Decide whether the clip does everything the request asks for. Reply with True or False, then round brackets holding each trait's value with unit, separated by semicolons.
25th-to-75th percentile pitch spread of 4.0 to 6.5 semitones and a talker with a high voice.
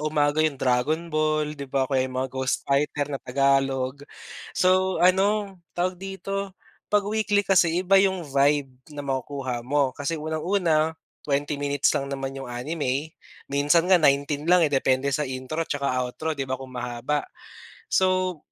False (4.3 semitones; 145 Hz)